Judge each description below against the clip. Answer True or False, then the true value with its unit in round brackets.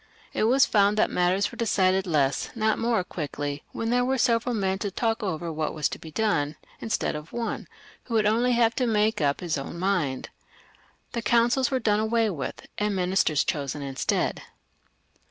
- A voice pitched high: True (205 Hz)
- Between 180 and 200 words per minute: True (190 wpm)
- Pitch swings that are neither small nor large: False (6.3 semitones)